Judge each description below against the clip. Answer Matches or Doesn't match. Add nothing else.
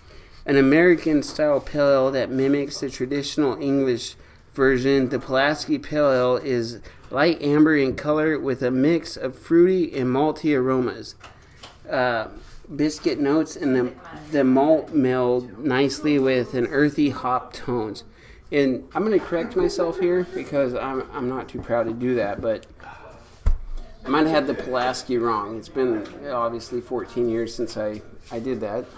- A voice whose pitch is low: Matches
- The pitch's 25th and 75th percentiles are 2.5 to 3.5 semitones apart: Matches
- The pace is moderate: Matches